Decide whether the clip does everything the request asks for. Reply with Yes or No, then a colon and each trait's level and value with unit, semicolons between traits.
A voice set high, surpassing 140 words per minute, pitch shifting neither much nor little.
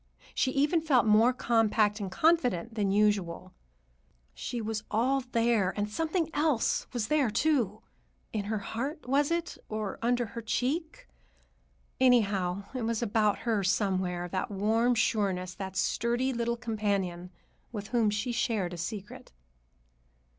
No: high, 225 Hz; slow, 135 wpm; average, 3.6 semitones